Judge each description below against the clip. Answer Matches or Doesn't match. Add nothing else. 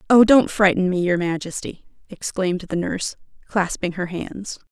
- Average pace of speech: Matches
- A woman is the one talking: Matches